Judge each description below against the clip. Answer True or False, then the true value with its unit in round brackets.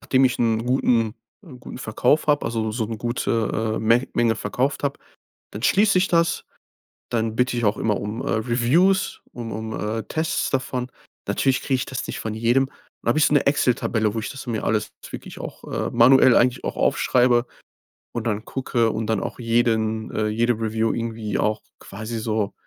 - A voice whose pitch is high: False (115 Hz)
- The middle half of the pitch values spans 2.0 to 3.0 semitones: True (2.5 semitones)